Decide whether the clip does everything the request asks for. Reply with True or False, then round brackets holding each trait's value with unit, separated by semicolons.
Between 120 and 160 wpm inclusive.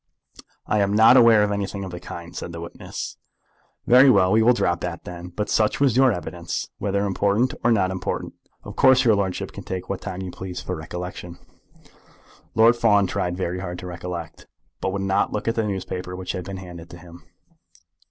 False (200 wpm)